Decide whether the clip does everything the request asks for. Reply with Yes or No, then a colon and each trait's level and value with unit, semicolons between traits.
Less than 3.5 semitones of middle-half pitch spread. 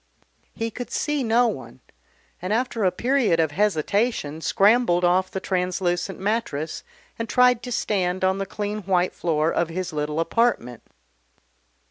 No: average, 4.9 semitones